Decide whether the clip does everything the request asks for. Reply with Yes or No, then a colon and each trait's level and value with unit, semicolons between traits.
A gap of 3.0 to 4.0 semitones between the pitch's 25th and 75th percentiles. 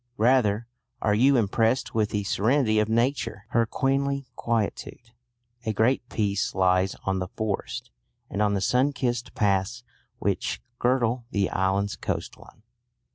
Yes: average, 3.6 semitones